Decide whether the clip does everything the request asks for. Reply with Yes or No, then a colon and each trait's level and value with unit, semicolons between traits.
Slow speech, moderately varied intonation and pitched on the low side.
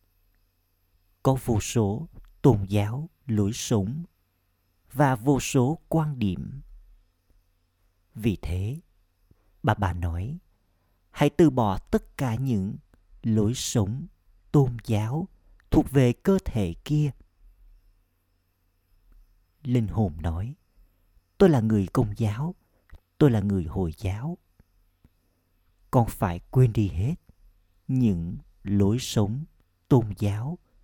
No: slow, 105 wpm; wide, 6.2 semitones; low, 100 Hz